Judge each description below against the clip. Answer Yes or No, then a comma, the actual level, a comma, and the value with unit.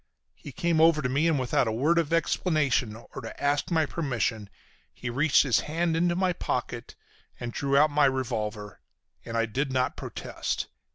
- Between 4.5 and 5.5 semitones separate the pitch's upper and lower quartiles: Yes, average, 5.0 semitones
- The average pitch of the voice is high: No, medium, 140 Hz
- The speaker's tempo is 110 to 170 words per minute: No, average, 180 wpm